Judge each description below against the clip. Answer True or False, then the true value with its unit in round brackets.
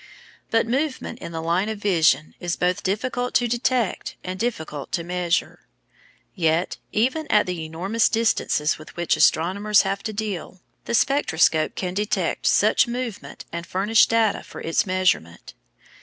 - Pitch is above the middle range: True (195 Hz)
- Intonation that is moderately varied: True (5.0 semitones)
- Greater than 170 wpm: False (150 wpm)